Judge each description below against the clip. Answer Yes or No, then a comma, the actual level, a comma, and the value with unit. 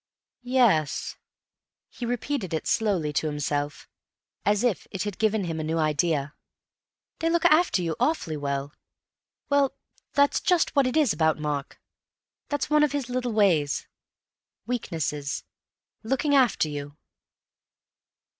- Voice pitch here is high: Yes, high, 195 Hz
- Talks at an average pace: No, slow, 130 wpm